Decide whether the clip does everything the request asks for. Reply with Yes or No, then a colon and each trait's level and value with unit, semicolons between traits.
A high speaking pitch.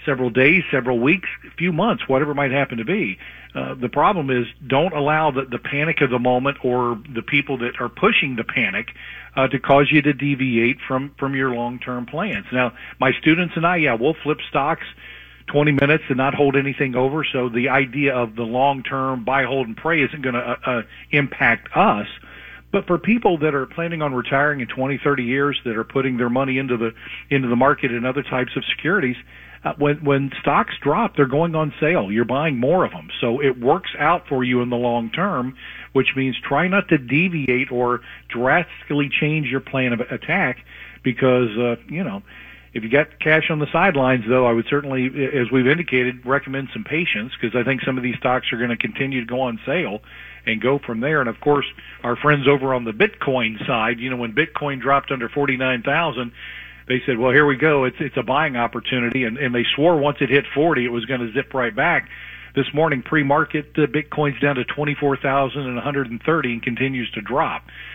No: low, 135 Hz